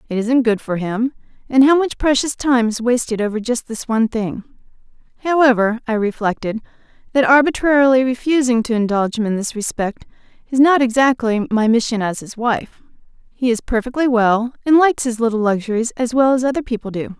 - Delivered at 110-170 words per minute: No, average, 180 wpm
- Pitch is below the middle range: No, high, 240 Hz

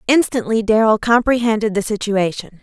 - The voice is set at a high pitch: Yes, high, 220 Hz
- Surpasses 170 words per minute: No, slow, 115 wpm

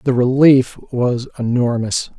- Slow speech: Yes, slow, 110 wpm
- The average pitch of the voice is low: Yes, low, 125 Hz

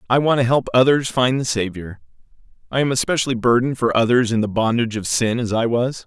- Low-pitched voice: Yes, low, 120 Hz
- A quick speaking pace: Yes, fast, 220 wpm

